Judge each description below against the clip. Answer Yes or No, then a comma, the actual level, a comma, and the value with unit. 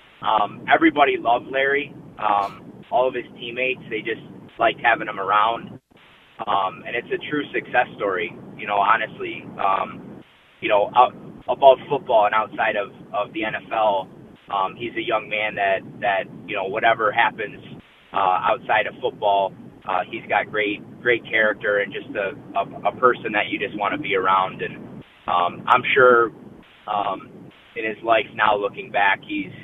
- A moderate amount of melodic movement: No, wide, 6.3 semitones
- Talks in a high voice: No, low, 110 Hz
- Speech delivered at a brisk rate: No, average, 165 wpm